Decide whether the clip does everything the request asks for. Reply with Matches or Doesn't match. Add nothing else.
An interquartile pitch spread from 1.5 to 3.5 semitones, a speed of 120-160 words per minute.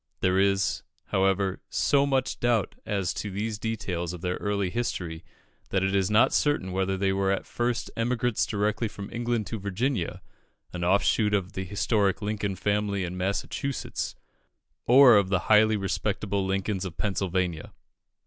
Matches